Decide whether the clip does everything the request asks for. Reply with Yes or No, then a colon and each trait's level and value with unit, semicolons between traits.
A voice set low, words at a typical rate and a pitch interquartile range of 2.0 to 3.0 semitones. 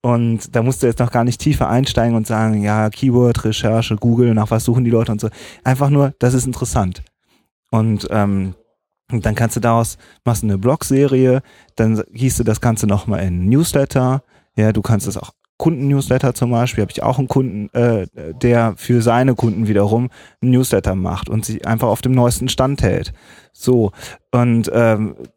Yes: low, 120 Hz; average, 180 wpm; narrow, 2.6 semitones